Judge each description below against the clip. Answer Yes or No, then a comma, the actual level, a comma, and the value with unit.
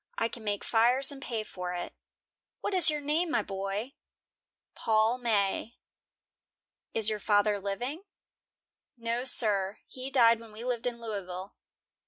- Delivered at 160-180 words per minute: No, average, 145 wpm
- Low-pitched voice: No, high, 230 Hz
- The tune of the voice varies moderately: Yes, average, 3.6 semitones